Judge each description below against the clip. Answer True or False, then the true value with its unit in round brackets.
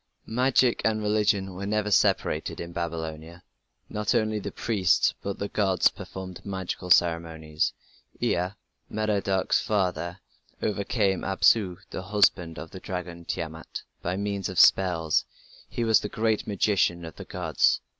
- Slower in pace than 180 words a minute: True (140 wpm)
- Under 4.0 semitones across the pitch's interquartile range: True (3.4 semitones)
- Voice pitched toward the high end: False (95 Hz)